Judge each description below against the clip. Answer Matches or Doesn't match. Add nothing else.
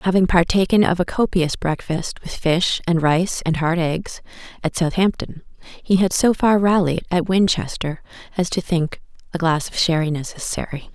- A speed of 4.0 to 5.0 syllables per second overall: Matches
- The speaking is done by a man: Doesn't match